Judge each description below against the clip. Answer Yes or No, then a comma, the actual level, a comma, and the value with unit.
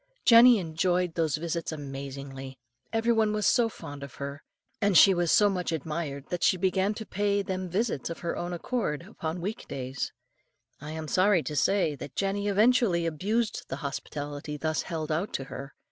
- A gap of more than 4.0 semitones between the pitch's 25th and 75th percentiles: Yes, wide, 5.4 semitones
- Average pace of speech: Yes, average, 175 wpm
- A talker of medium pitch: Yes, medium, 170 Hz